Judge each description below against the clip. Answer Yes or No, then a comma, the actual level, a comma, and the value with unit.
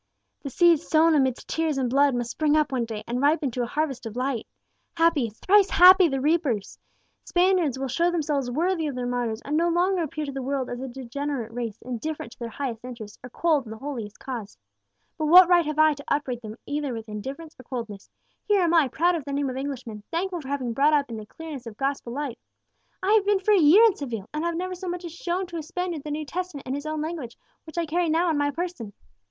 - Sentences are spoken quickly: Yes, fast, 250 wpm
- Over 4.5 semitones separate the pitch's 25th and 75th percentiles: Yes, average, 5.2 semitones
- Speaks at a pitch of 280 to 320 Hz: Yes, very high, 285 Hz